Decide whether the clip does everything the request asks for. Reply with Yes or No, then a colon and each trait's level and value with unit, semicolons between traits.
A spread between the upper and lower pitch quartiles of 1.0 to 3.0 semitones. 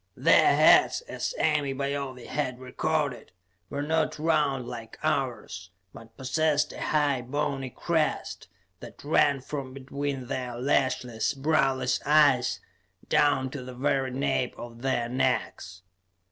Yes: narrow, 2.6 semitones